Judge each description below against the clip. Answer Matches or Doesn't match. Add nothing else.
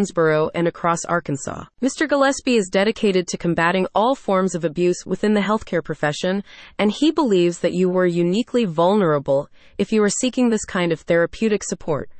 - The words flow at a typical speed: Matches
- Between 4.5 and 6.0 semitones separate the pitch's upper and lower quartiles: Doesn't match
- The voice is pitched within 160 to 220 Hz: Matches